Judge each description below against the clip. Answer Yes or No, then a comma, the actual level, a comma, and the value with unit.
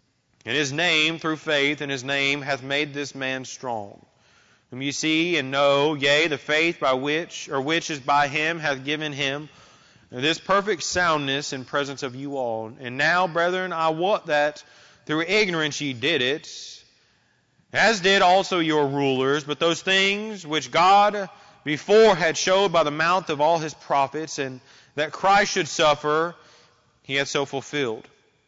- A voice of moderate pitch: Yes, medium, 150 Hz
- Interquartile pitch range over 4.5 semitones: No, average, 3.0 semitones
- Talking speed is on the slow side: No, average, 165 wpm